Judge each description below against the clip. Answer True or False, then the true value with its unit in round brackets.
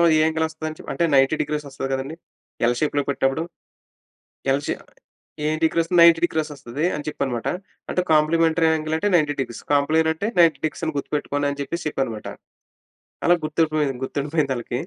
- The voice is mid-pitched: True (150 Hz)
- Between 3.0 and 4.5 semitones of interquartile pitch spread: False (2.4 semitones)